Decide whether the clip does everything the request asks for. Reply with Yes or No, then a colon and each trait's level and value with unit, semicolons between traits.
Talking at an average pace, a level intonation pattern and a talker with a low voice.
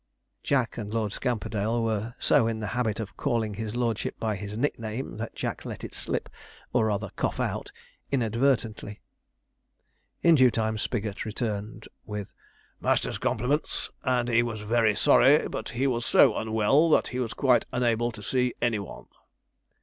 Yes: average, 160 wpm; narrow, 2.3 semitones; low, 115 Hz